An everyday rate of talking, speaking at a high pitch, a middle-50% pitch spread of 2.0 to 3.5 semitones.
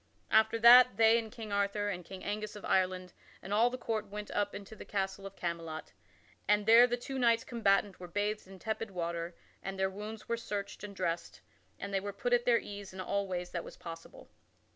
No: fast, 220 wpm; high, 205 Hz; average, 2.8 semitones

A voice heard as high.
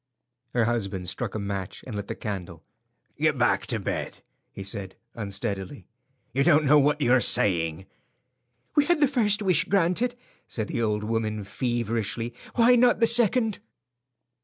No: low, 115 Hz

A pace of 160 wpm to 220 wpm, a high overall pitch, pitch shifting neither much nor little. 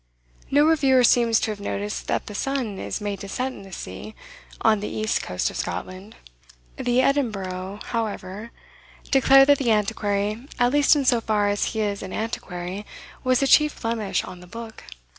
Yes: average, 180 wpm; high, 220 Hz; average, 4.1 semitones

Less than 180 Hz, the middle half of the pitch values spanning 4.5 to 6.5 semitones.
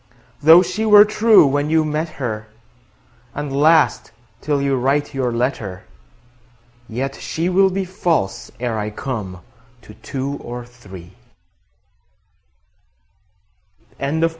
Yes: medium, 140 Hz; average, 5.1 semitones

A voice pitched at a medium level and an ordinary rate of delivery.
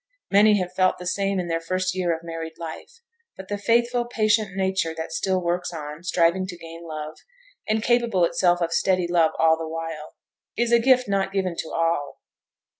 Yes: medium, 180 Hz; average, 190 wpm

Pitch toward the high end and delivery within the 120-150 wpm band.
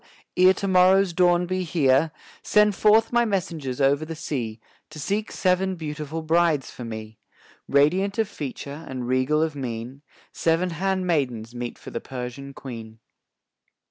No: medium, 155 Hz; average, 145 wpm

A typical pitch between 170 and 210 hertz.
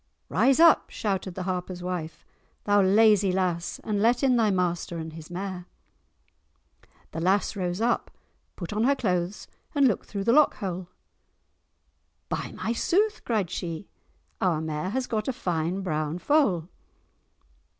Yes: high, 190 Hz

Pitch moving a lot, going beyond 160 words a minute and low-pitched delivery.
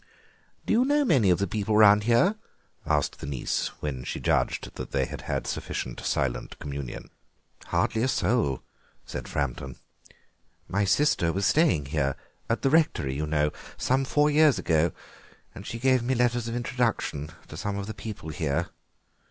Yes: wide, 8.9 semitones; average, 170 wpm; low, 105 Hz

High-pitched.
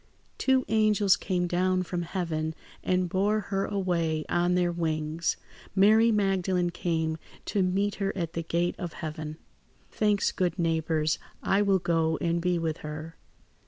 No: medium, 175 Hz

